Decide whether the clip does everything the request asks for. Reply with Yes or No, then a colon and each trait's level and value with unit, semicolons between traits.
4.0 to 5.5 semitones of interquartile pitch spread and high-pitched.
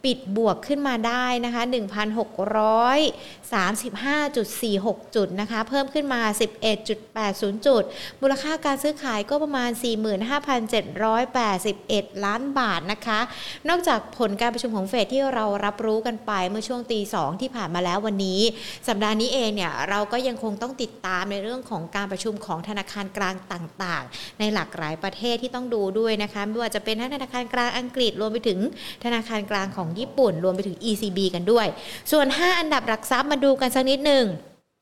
No: average, 3.5 semitones; high, 220 Hz